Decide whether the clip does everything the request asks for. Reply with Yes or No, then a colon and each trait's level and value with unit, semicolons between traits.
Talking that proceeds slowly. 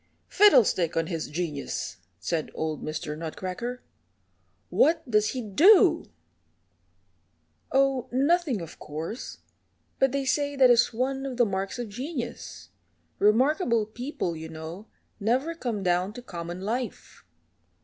Yes: slow, 125 wpm